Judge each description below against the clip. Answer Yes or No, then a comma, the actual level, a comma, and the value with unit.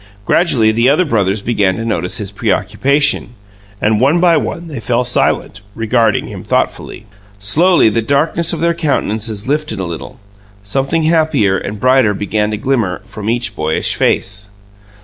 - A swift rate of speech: No, average, 155 wpm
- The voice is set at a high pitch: No, low, 115 Hz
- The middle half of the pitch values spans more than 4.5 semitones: Yes, wide, 5.6 semitones